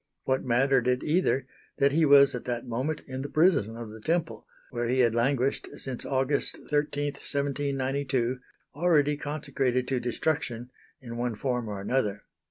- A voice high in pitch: No, low, 130 Hz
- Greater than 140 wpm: Yes, average, 160 wpm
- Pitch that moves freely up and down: No, average, 2.9 semitones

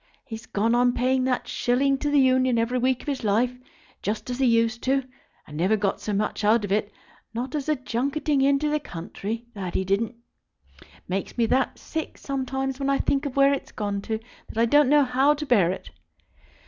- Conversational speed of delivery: No, fast, 215 wpm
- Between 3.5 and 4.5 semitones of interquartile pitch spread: Yes, average, 3.9 semitones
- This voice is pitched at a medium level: No, very high, 250 Hz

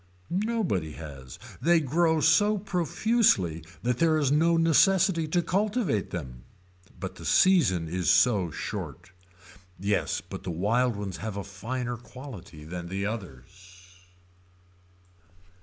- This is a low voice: Yes, low, 115 Hz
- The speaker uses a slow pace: Yes, slow, 125 wpm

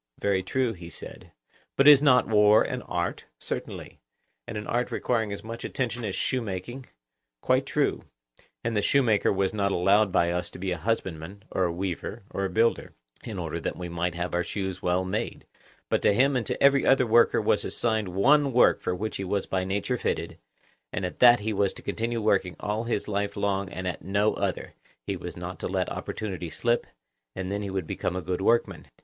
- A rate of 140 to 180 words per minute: No, fast, 205 wpm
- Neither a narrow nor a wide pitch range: Yes, average, 3.9 semitones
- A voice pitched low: Yes, low, 100 Hz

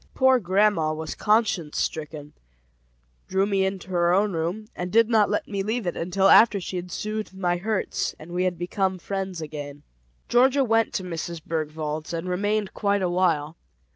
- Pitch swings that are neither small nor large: Yes, average, 3.9 semitones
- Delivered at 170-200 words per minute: Yes, average, 175 wpm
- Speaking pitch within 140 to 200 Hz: Yes, medium, 185 Hz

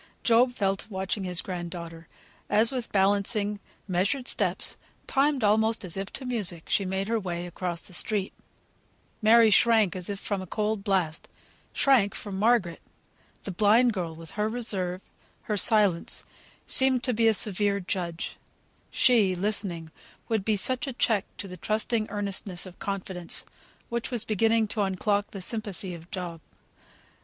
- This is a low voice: No, high, 200 Hz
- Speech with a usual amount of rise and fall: Yes, average, 3.4 semitones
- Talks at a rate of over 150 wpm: Yes, average, 160 wpm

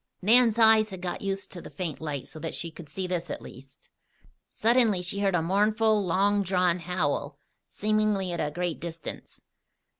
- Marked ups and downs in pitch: No, average, 3.9 semitones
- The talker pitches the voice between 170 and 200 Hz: Yes, medium, 185 Hz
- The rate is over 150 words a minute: Yes, average, 180 wpm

